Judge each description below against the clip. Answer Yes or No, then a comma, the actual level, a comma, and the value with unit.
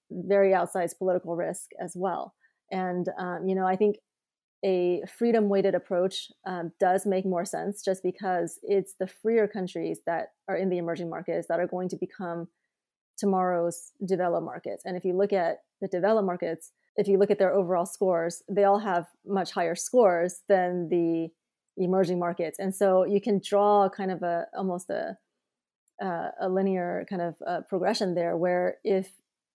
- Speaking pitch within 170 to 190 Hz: Yes, medium, 185 Hz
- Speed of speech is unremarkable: Yes, average, 175 wpm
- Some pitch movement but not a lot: No, narrow, 1.8 semitones